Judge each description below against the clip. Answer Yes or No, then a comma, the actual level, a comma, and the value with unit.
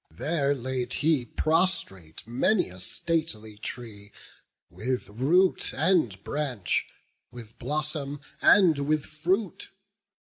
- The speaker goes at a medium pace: No, slow, 100 wpm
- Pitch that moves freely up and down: Yes, wide, 6.3 semitones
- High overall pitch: No, medium, 140 Hz